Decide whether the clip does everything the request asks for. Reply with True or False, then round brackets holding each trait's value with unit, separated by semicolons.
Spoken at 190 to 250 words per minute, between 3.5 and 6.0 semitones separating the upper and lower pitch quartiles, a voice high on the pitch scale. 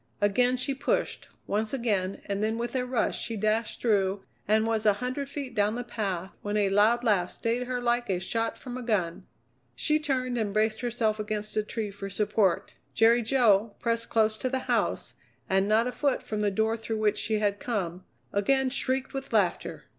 False (200 wpm; 3.1 semitones; 220 Hz)